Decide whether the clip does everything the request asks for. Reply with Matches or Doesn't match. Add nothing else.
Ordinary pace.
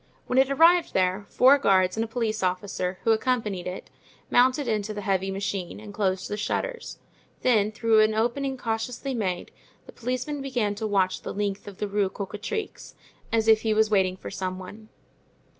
Matches